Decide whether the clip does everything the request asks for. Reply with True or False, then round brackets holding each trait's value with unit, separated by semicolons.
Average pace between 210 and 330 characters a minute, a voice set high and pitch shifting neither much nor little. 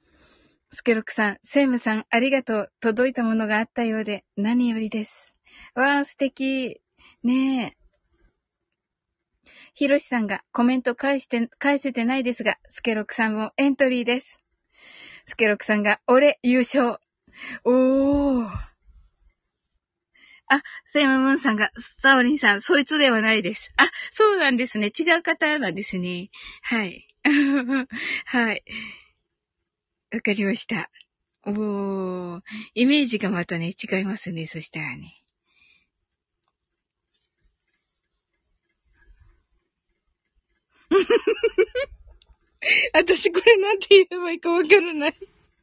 True (230 characters per minute; 245 Hz; 4.9 semitones)